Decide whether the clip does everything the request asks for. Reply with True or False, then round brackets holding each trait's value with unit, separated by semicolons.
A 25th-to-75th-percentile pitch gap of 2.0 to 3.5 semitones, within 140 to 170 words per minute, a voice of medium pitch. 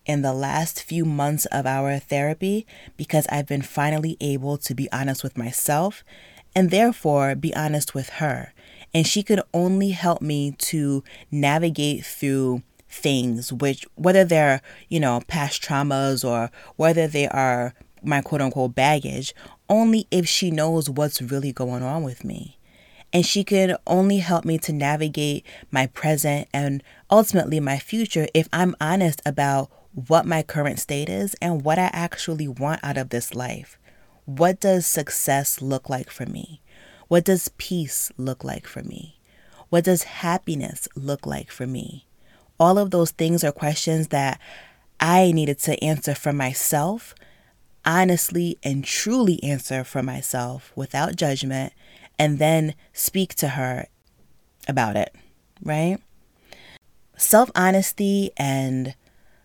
False (4.0 semitones; 145 wpm; 150 Hz)